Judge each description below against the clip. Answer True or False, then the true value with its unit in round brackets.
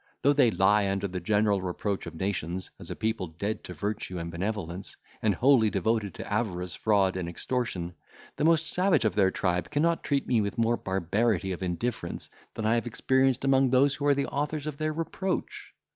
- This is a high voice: False (110 Hz)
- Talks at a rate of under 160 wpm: False (195 wpm)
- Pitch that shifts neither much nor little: False (6.0 semitones)